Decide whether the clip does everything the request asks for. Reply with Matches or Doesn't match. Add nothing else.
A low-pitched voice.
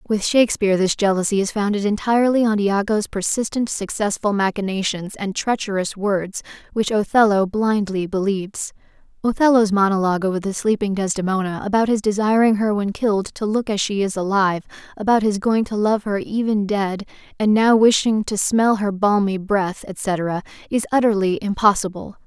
Doesn't match